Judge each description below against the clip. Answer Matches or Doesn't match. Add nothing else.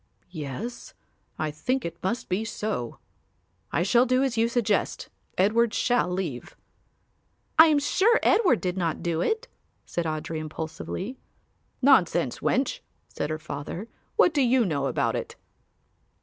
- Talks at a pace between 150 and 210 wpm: Doesn't match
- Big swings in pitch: Matches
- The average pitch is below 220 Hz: Matches